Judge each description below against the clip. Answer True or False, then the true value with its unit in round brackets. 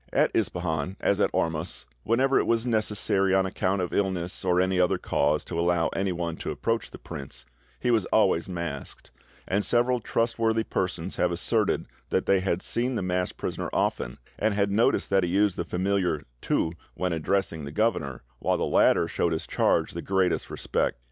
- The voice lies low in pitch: True (95 Hz)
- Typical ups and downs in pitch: True (3.5 semitones)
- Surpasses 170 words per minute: True (180 wpm)